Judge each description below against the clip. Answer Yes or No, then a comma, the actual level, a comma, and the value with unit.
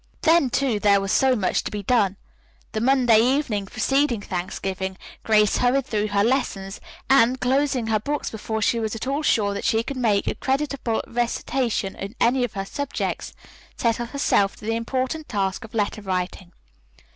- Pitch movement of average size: Yes, average, 4.3 semitones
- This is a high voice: Yes, high, 225 Hz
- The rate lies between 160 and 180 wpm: Yes, average, 175 wpm